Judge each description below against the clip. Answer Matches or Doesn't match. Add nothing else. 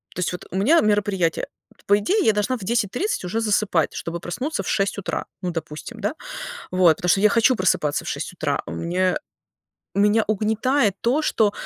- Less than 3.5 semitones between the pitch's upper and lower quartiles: Doesn't match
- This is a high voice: Matches